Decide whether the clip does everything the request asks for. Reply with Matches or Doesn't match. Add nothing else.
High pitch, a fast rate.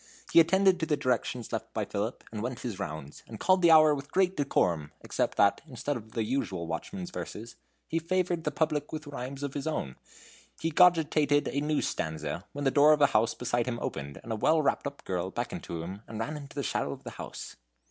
Doesn't match